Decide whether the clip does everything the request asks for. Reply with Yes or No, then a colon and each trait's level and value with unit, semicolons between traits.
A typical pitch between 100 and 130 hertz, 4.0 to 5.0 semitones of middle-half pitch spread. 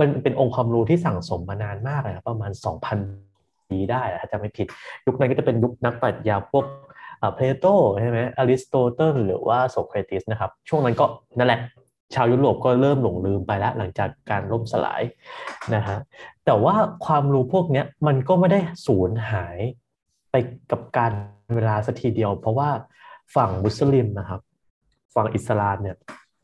Yes: low, 115 Hz; average, 4.5 semitones